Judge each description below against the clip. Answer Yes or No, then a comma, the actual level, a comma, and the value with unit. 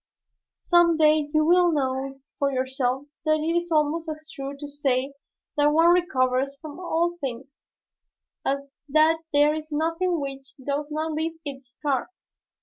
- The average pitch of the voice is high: Yes, very high, 295 Hz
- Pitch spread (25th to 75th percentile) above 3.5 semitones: No, average, 2.9 semitones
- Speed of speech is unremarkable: Yes, average, 150 wpm